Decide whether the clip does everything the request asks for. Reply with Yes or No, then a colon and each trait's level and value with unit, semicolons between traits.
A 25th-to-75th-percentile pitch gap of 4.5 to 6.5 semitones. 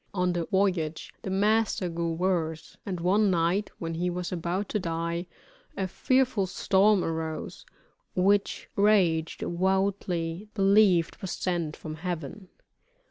No: average, 2.8 semitones